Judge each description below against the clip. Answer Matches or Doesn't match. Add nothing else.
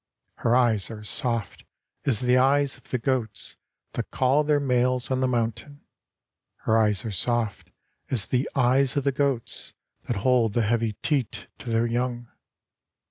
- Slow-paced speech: Doesn't match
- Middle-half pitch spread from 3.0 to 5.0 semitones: Doesn't match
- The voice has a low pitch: Matches